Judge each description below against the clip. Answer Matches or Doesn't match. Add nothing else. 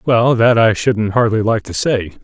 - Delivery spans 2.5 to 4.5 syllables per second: Matches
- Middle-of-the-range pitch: Doesn't match